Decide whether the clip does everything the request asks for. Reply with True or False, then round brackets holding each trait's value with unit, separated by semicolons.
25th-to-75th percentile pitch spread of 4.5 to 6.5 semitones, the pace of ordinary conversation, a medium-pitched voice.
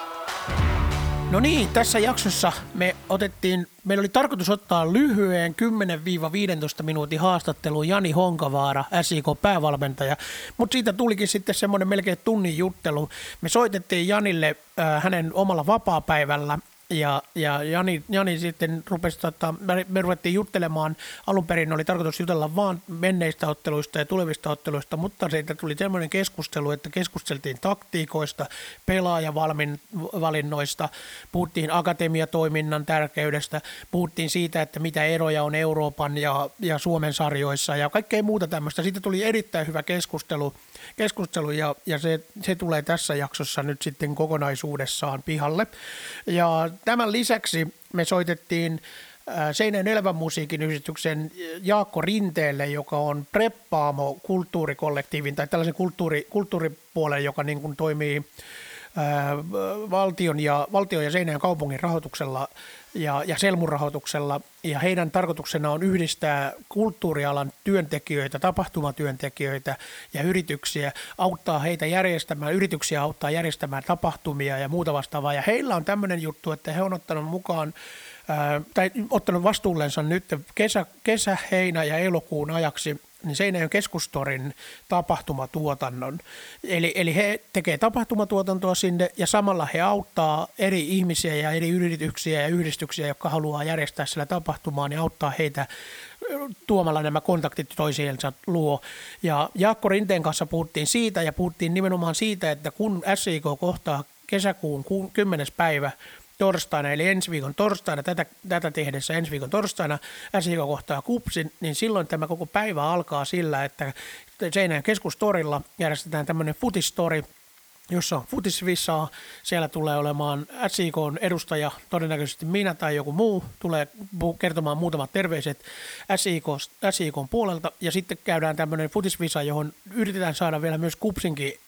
False (3.8 semitones; 130 wpm; 165 Hz)